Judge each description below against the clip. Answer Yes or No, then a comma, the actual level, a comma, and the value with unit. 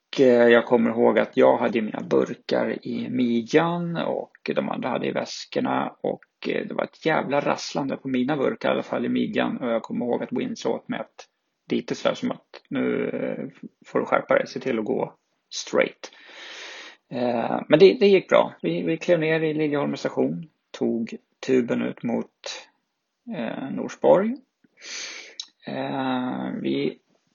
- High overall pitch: No, low, 135 Hz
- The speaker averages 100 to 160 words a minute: Yes, average, 155 wpm